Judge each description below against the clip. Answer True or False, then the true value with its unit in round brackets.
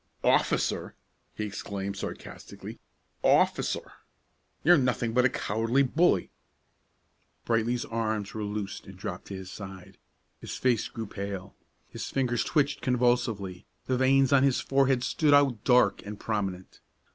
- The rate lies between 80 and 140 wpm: True (135 wpm)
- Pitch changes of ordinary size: True (4.3 semitones)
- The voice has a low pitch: True (115 Hz)